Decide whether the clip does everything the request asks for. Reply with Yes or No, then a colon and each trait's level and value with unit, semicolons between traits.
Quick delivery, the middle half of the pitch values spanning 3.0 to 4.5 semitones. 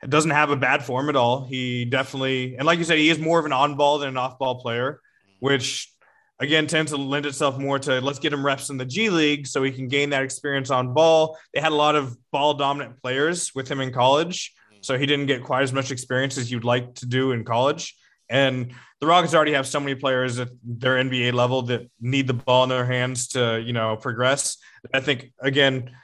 No: fast, 230 wpm; narrow, 2.4 semitones